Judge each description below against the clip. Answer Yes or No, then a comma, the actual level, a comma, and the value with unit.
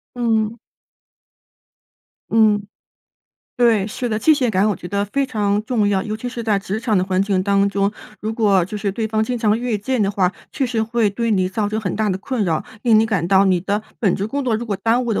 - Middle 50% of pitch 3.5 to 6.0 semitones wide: No, narrow, 2.5 semitones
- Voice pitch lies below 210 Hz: No, high, 215 Hz